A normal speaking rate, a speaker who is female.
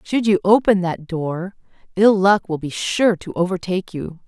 Yes: average, 180 wpm; female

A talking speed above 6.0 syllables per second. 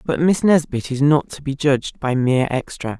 No: 5.1 syllables/s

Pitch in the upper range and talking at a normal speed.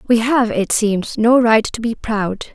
No: high, 225 Hz; fast, 210 wpm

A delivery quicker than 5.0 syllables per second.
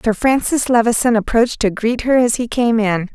Yes: 5.3 syllables/s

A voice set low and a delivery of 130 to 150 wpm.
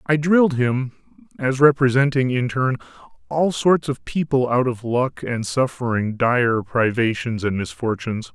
Yes: low, 125 Hz; average, 145 wpm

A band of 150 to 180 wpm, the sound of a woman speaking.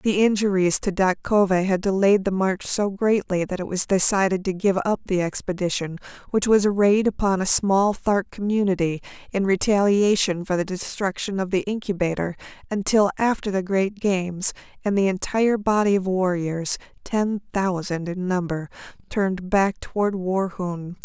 Yes: average, 160 wpm; female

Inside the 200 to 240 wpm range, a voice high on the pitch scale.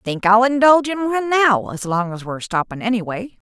Yes: fast, 205 wpm; high, 225 Hz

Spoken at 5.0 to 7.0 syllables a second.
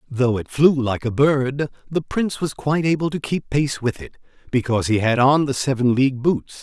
Yes: 5.3 syllables/s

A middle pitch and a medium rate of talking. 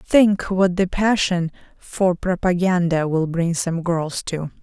Yes: medium, 175 Hz; average, 145 wpm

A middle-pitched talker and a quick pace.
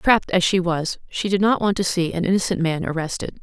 Yes: medium, 180 Hz; fast, 245 wpm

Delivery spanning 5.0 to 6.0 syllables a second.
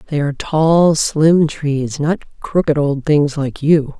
No: 3.6 syllables/s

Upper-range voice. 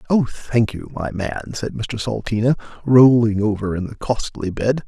No: low, 115 Hz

